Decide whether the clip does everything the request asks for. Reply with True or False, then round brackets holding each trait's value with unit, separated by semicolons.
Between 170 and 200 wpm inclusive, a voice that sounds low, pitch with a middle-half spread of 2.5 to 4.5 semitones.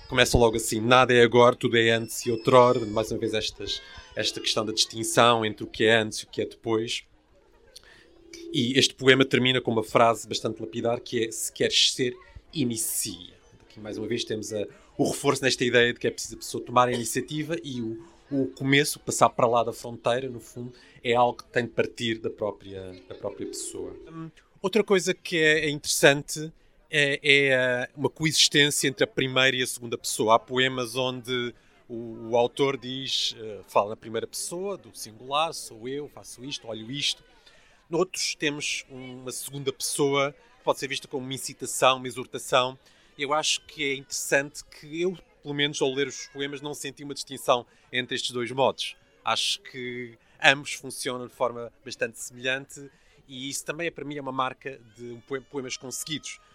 True (185 wpm; 130 Hz; 3.2 semitones)